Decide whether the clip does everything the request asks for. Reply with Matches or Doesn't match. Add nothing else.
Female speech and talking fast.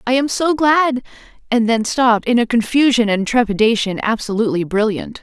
Doesn't match